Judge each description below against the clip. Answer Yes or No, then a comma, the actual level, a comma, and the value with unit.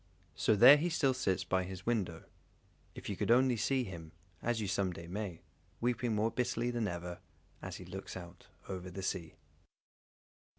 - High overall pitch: No, low, 100 Hz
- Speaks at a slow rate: No, average, 175 wpm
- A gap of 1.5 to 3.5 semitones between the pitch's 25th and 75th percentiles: No, average, 4.8 semitones